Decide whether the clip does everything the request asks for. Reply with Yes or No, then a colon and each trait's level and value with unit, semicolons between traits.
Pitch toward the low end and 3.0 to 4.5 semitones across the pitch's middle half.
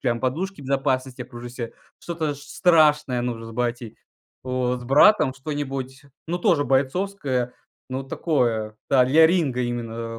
Yes: low, 130 Hz; average, 3.4 semitones